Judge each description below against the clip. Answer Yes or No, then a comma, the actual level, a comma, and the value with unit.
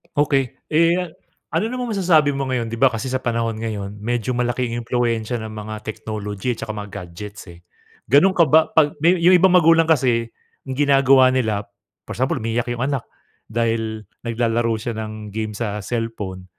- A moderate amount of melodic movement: Yes, average, 4.1 semitones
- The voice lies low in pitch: Yes, low, 120 Hz